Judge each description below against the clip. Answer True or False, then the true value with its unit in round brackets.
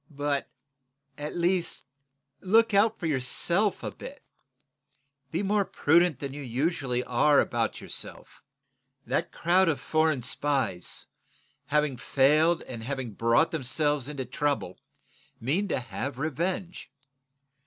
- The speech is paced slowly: True (120 wpm)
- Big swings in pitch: False (4.6 semitones)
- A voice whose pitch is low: False (145 Hz)